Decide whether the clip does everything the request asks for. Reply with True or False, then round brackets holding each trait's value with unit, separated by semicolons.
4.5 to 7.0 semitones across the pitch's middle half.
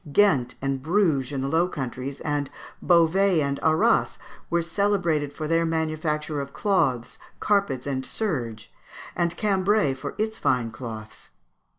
True (5.1 semitones)